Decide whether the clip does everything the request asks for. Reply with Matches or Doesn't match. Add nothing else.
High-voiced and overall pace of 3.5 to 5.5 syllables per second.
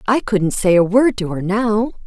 Matches